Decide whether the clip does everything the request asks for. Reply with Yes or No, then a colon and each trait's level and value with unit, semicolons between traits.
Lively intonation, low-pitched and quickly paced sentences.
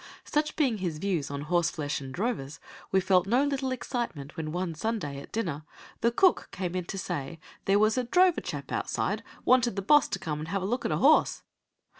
No: wide, 7.6 semitones; high, 190 Hz; fast, 210 wpm